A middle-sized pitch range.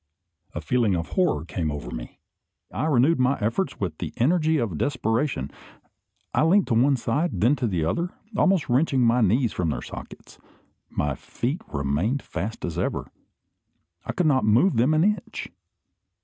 No: wide, 9.0 semitones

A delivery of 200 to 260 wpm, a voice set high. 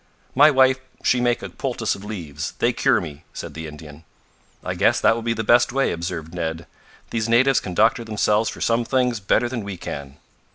No: fast, 205 wpm; low, 110 Hz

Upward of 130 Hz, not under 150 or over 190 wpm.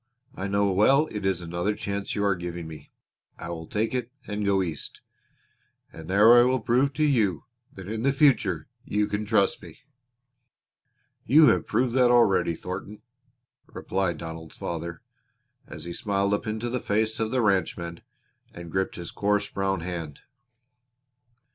No: low, 100 Hz; average, 160 wpm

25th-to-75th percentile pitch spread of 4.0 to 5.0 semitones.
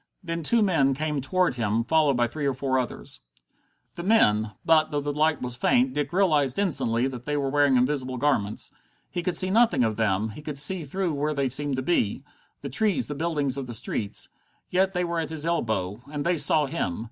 Yes: average, 4.6 semitones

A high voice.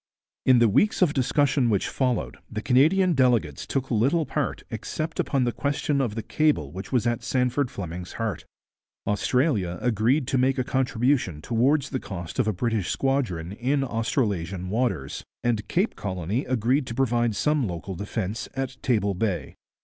No: low, 120 Hz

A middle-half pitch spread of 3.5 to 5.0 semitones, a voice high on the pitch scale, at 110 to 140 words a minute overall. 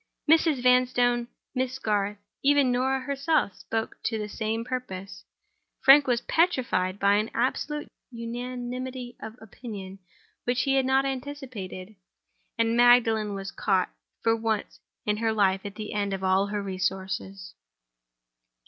Yes: average, 4.1 semitones; high, 230 Hz; slow, 135 wpm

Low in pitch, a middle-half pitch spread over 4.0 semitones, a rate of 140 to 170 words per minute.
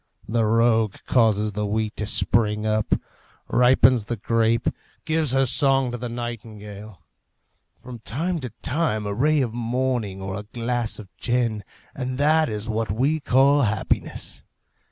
No: low, 115 Hz; average, 3.1 semitones; average, 150 wpm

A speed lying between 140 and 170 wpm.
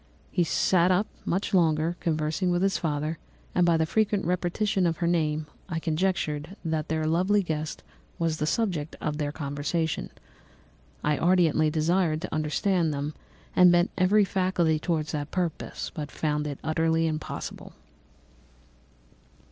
Yes: average, 145 wpm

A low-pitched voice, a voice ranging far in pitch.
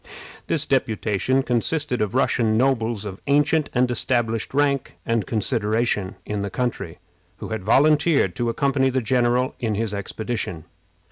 No: low, 120 Hz; average, 3.7 semitones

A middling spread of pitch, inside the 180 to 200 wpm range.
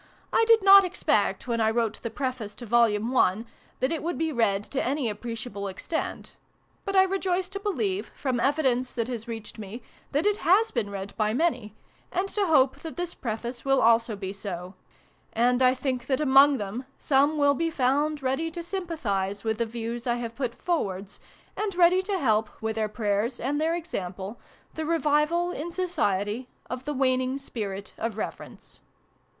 No: wide, 6.4 semitones; average, 185 wpm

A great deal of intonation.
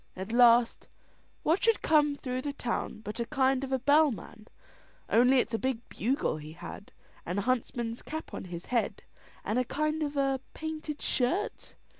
No: average, 4.1 semitones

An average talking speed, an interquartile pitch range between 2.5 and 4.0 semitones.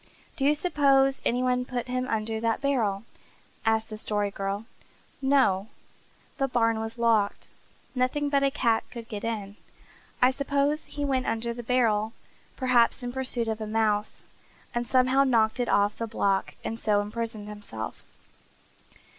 Yes: average, 155 wpm; average, 3.2 semitones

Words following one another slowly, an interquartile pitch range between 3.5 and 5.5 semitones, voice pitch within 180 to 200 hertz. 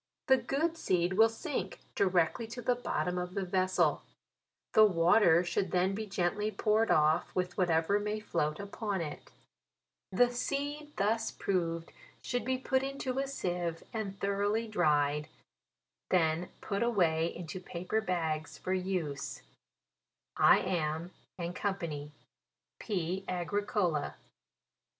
Yes: slow, 125 wpm; average, 4.3 semitones; medium, 185 Hz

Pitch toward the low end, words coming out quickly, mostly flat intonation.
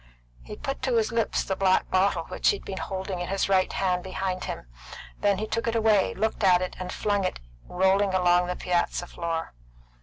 No: high, 190 Hz; fast, 210 wpm; narrow, 2.3 semitones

